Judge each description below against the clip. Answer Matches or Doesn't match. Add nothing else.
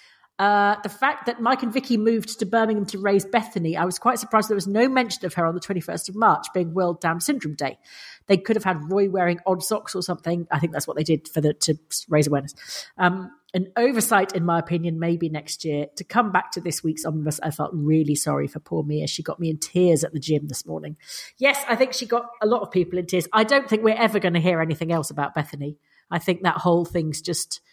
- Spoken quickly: Matches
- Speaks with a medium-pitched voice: Matches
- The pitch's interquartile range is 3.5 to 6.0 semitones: Matches